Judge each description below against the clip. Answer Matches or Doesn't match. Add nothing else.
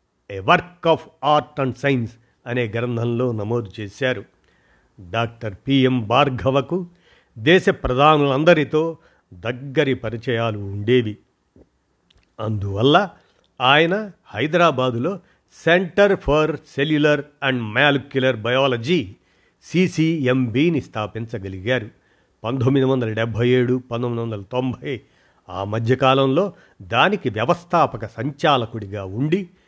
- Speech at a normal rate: Matches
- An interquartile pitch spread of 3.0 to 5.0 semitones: Matches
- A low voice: Matches